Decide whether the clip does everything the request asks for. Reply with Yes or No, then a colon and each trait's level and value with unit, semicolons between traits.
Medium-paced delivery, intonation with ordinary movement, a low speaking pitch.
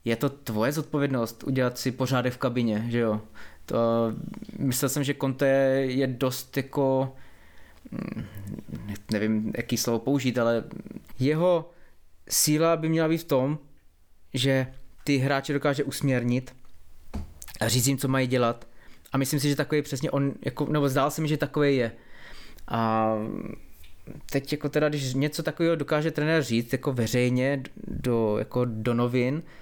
Yes: average, 150 wpm; average, 3.8 semitones; low, 130 Hz